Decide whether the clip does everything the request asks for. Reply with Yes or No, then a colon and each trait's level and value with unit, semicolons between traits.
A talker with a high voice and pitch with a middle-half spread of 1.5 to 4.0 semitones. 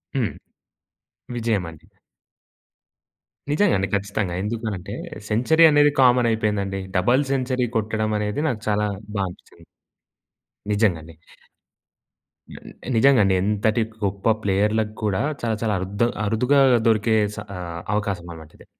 No: low, 105 Hz; average, 3.0 semitones